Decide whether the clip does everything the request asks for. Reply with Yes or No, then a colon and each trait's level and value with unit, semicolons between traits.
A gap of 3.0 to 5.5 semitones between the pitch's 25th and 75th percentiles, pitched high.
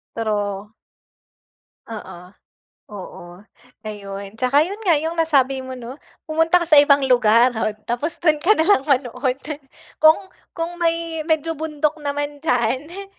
Yes: average, 5.2 semitones; very high, 285 Hz